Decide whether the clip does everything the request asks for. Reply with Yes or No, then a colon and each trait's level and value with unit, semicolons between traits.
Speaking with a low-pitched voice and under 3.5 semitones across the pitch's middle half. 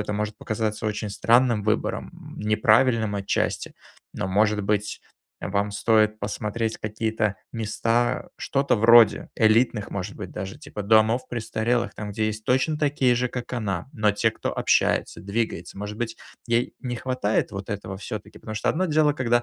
Yes: low, 110 Hz; narrow, 2.4 semitones